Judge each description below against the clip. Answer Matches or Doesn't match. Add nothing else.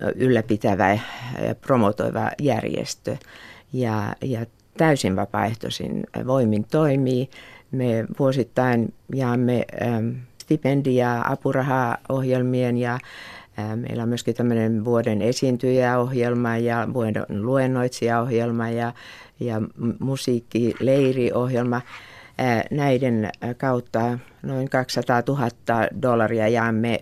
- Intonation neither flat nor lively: Doesn't match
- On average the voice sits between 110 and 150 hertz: Matches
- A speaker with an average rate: Doesn't match